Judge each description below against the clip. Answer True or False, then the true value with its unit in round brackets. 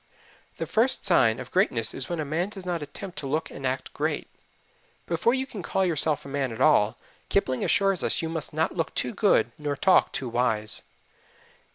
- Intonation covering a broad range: True (6.1 semitones)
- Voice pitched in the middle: True (155 Hz)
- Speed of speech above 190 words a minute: True (200 wpm)